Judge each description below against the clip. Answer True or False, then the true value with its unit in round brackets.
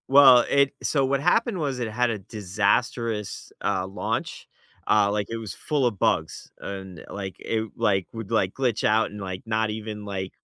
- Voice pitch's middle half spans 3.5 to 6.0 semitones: True (3.9 semitones)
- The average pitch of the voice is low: True (110 Hz)